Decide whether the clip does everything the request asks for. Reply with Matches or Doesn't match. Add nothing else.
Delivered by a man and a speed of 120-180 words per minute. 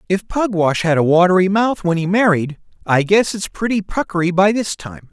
Doesn't match